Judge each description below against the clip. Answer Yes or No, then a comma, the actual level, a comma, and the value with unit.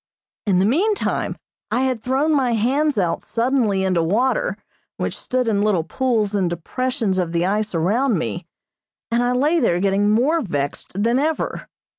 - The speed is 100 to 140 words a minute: No, average, 165 wpm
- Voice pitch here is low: No, high, 225 Hz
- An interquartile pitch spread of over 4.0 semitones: Yes, wide, 5.6 semitones